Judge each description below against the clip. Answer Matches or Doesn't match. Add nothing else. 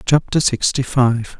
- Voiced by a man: Matches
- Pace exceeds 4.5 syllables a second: Doesn't match